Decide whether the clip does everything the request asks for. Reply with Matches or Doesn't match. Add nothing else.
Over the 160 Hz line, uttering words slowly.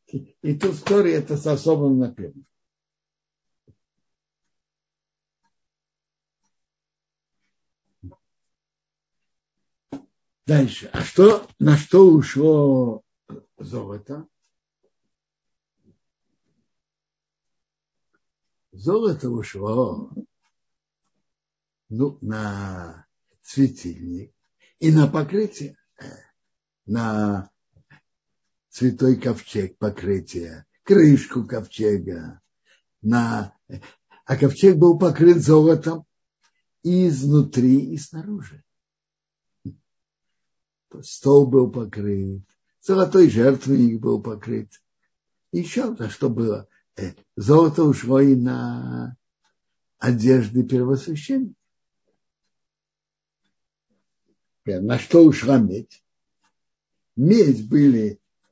Doesn't match